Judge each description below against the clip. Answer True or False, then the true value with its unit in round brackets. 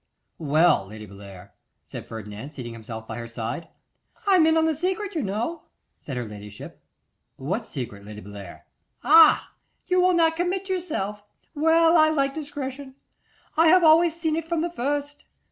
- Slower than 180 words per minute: True (160 wpm)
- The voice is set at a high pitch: True (275 Hz)